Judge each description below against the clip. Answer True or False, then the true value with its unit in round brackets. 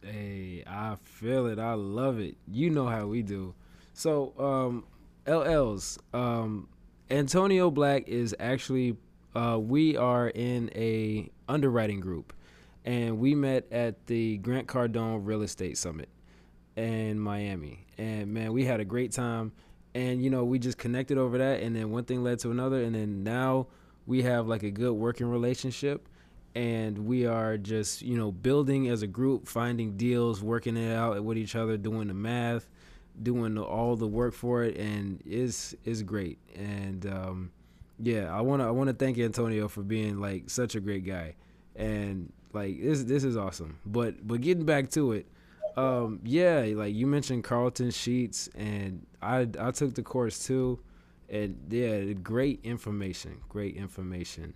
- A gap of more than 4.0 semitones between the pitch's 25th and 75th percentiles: False (3.7 semitones)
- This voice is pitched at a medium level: False (115 Hz)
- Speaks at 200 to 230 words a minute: False (165 wpm)